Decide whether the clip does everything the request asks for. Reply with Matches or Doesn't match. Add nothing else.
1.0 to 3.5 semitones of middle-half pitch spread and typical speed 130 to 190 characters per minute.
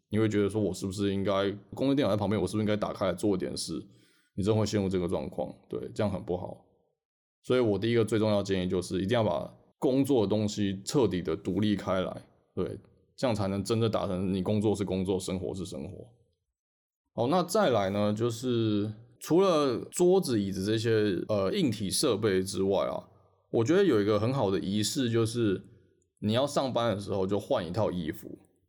Doesn't match